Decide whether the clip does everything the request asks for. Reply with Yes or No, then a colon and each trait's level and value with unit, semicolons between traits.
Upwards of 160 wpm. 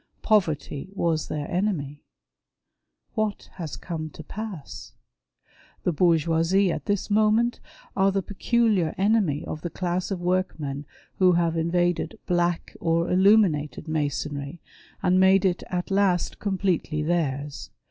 No: slow, 135 wpm